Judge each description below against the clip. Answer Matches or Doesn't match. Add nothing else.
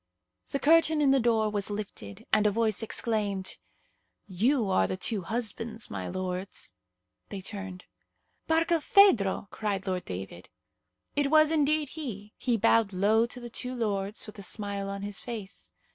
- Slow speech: Doesn't match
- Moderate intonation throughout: Matches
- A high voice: Matches